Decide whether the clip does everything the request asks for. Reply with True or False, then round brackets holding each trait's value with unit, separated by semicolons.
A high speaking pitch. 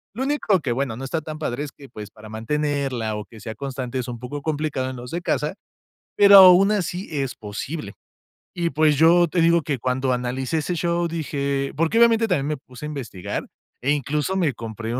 False (145 Hz)